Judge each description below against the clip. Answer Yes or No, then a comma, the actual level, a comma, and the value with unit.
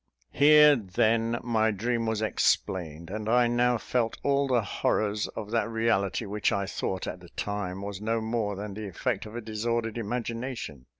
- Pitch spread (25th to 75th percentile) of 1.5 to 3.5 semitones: Yes, narrow, 2.6 semitones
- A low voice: Yes, low, 110 Hz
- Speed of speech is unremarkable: Yes, average, 175 wpm